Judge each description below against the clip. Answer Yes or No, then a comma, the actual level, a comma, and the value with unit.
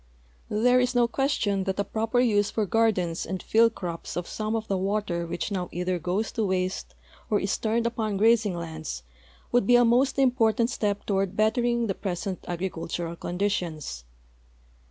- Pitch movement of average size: Yes, average, 4.1 semitones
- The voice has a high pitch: Yes, high, 205 Hz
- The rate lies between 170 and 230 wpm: Yes, average, 175 wpm